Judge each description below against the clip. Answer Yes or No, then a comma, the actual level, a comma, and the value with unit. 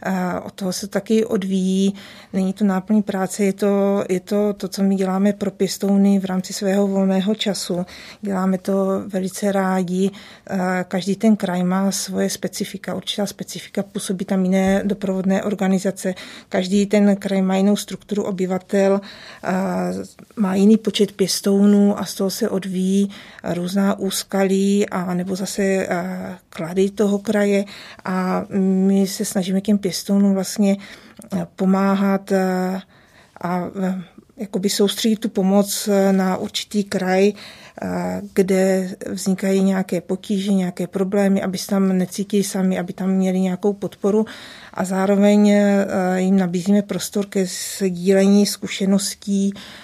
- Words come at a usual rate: Yes, average, 125 wpm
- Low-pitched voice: No, high, 195 Hz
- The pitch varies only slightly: Yes, narrow, 1.3 semitones